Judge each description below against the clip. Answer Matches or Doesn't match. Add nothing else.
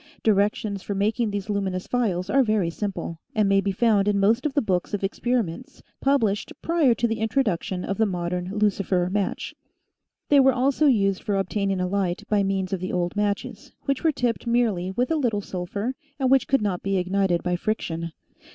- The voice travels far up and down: Doesn't match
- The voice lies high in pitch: Matches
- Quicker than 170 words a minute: Matches